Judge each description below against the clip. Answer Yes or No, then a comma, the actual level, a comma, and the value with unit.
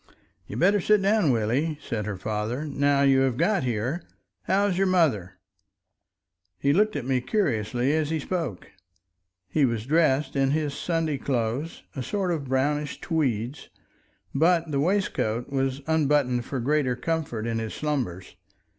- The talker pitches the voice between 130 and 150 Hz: Yes, medium, 140 Hz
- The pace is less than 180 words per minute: Yes, average, 150 wpm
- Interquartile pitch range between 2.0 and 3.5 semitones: No, average, 4.9 semitones